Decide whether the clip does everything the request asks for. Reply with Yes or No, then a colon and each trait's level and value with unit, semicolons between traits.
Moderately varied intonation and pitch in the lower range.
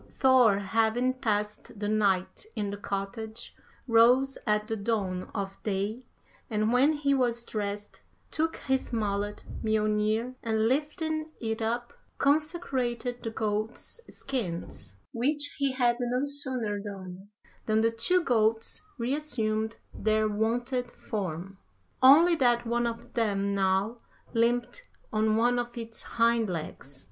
No: average, 3.1 semitones; high, 225 Hz